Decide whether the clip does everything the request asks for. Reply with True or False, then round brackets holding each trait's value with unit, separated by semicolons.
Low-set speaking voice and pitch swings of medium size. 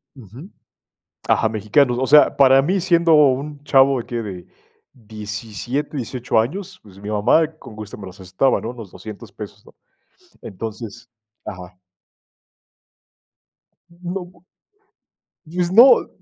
False (125 Hz; 6.0 semitones)